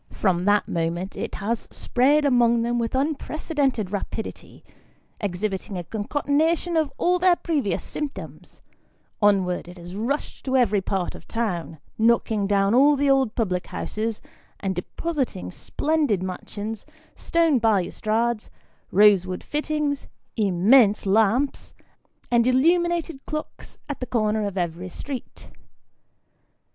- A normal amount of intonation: No, wide, 6.4 semitones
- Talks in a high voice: Yes, high, 225 Hz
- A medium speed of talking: No, slow, 120 wpm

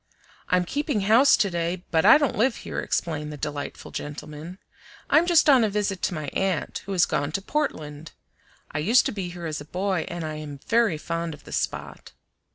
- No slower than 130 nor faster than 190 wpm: No, fast, 205 wpm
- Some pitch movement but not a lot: No, wide, 5.7 semitones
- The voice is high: No, medium, 175 Hz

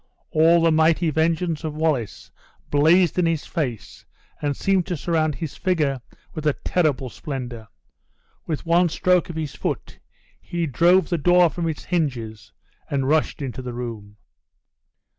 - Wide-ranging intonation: No, average, 3.9 semitones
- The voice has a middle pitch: Yes, medium, 155 Hz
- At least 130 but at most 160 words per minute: Yes, average, 150 wpm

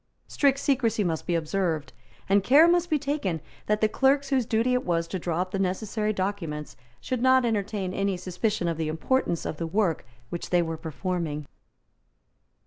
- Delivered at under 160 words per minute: No, average, 180 wpm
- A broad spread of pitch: Yes, wide, 6.3 semitones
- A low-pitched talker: No, high, 195 Hz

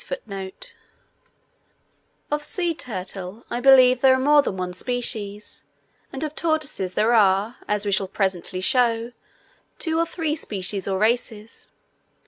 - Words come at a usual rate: No, slow, 130 wpm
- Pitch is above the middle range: Yes, high, 230 Hz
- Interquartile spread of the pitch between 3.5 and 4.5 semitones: No, wide, 5.6 semitones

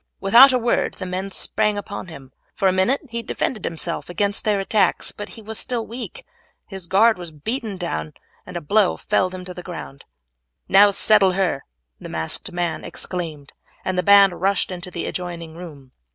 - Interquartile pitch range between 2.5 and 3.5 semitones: Yes, average, 3.2 semitones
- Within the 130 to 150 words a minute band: No, average, 185 wpm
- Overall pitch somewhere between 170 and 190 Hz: Yes, medium, 185 Hz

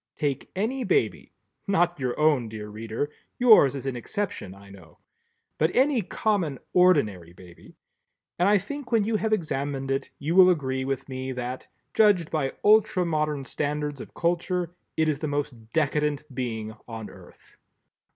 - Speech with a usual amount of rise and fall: No, wide, 6.2 semitones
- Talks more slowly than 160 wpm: Yes, average, 150 wpm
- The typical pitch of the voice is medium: Yes, medium, 150 Hz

